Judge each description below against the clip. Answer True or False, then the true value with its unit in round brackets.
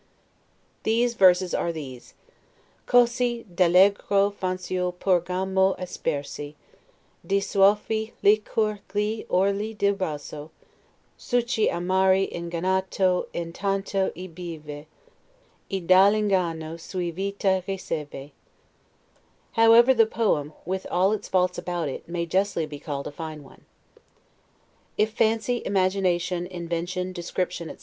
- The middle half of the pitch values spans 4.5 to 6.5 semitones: False (2.9 semitones)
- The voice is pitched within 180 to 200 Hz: True (185 Hz)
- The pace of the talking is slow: True (110 wpm)